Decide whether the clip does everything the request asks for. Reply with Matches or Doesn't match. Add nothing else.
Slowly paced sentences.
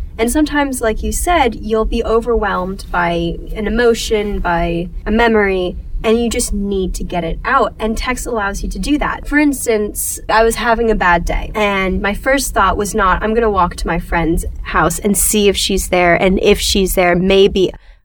Doesn't match